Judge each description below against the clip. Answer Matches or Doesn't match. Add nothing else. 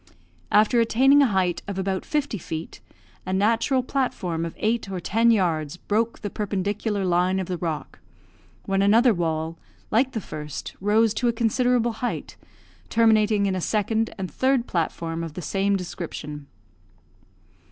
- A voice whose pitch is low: Doesn't match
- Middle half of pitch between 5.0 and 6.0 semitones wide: Doesn't match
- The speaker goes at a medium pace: Matches